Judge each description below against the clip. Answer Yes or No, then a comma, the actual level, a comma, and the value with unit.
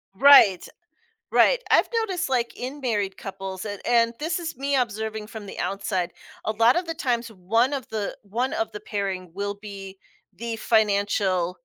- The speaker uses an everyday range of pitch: Yes, average, 4.5 semitones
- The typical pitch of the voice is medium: No, high, 220 Hz